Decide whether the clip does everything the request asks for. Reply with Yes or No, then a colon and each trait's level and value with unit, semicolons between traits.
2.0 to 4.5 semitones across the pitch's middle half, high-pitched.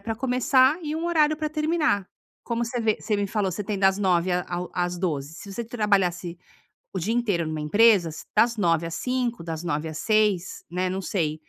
No: average, 5.3 semitones; high, 200 Hz